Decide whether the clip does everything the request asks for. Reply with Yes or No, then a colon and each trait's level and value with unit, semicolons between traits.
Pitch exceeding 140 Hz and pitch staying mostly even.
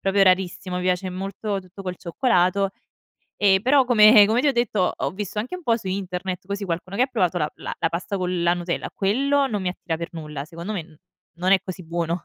No: high, 190 Hz; average, 3.0 semitones